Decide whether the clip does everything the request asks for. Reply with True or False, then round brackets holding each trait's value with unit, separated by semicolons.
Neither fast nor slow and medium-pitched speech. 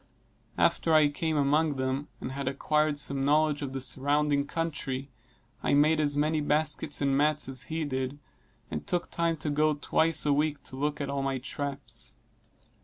True (180 wpm; 145 Hz)